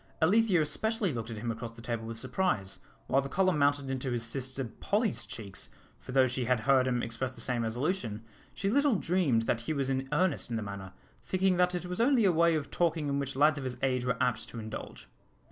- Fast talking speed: Yes, fast, 230 wpm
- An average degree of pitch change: No, wide, 7.0 semitones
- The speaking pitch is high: No, low, 135 Hz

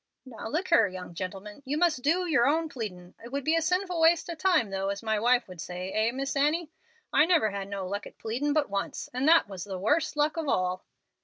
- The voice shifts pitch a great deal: Yes, wide, 7.9 semitones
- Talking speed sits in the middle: No, fast, 240 wpm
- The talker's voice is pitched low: No, very high, 250 Hz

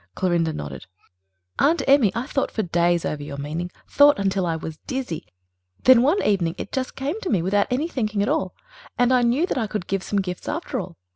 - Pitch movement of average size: No, wide, 7.3 semitones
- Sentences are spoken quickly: Yes, fast, 220 wpm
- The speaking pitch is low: No, high, 205 Hz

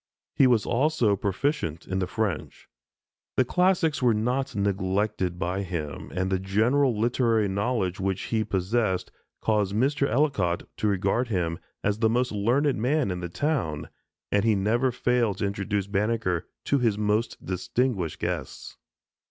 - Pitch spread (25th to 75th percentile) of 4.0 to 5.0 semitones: Yes, average, 4.5 semitones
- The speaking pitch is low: Yes, low, 105 Hz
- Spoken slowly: No, average, 150 wpm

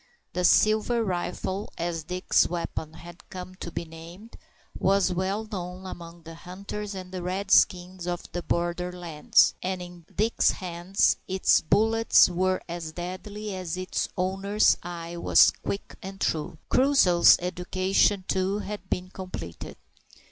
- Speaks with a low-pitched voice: No, medium, 185 Hz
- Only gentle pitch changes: Yes, narrow, 2.0 semitones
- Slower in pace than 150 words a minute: Yes, average, 140 wpm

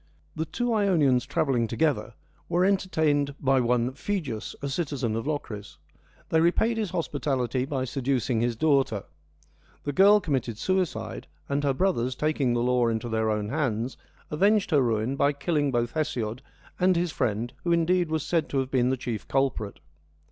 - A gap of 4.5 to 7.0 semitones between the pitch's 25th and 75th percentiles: Yes, average, 5.0 semitones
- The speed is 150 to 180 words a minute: Yes, average, 165 wpm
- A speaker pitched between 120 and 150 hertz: Yes, medium, 140 Hz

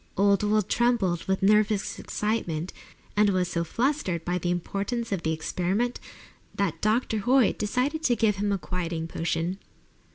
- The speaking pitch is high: Yes, high, 200 Hz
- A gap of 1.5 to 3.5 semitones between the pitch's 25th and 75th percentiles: No, average, 3.9 semitones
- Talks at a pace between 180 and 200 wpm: No, average, 155 wpm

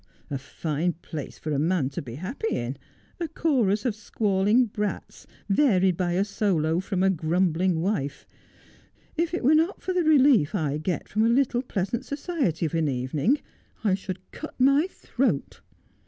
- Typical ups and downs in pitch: No, wide, 7.7 semitones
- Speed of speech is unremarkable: Yes, average, 170 wpm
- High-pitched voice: Yes, high, 195 Hz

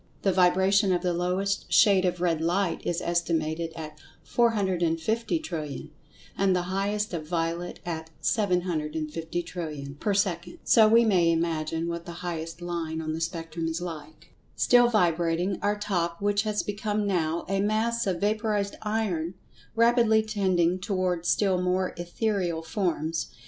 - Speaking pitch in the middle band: Yes, medium, 180 Hz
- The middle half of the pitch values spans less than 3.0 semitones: No, average, 3.5 semitones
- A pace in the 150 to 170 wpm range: No, average, 140 wpm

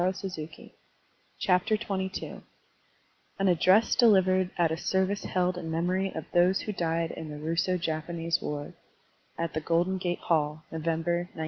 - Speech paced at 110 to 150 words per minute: Yes, average, 145 wpm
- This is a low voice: No, medium, 175 Hz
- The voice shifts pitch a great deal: No, narrow, 2.5 semitones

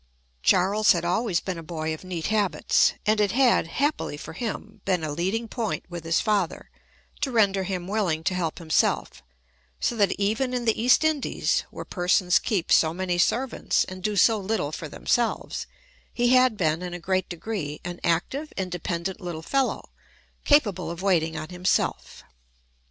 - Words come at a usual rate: Yes, average, 170 wpm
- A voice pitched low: No, medium, 185 Hz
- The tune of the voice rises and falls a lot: No, average, 4.4 semitones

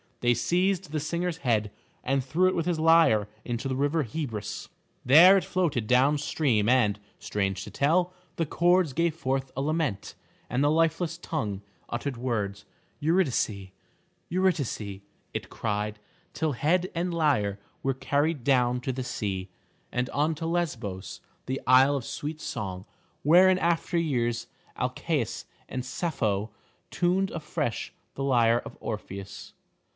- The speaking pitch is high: No, low, 135 Hz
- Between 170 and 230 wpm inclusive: No, average, 145 wpm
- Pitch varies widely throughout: Yes, wide, 6.2 semitones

